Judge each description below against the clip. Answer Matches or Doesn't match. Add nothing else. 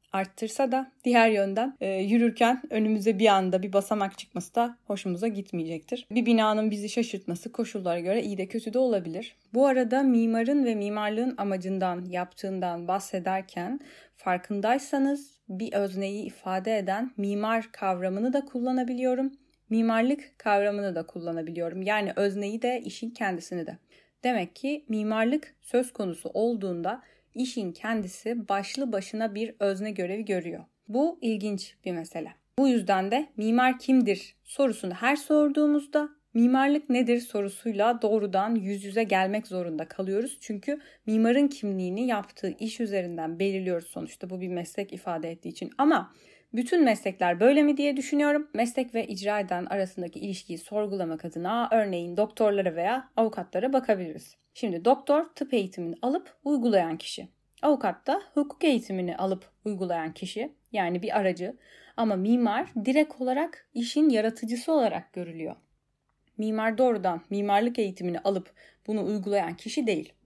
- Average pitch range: Matches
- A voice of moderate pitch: Doesn't match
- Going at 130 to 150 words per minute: Matches